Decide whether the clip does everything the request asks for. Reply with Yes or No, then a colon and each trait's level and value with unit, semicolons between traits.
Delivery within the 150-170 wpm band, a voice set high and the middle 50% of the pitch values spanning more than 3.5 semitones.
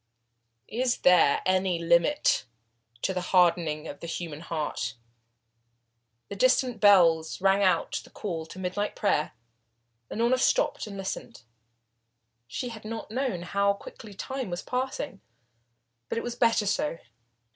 No: slow, 135 wpm; high, 195 Hz; average, 5.0 semitones